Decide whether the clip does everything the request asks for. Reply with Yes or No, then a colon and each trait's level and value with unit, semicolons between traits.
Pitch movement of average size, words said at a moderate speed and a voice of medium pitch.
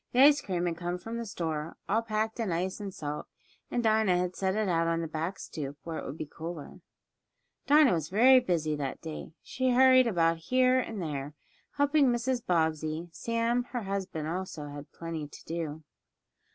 No: wide, 6.4 semitones; average, 190 wpm; medium, 180 Hz